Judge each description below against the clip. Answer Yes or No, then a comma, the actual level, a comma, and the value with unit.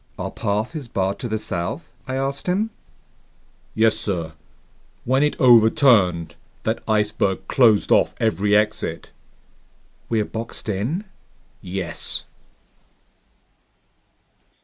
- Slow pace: Yes, slow, 105 wpm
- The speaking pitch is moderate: No, low, 110 Hz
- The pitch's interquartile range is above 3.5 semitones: Yes, average, 4.3 semitones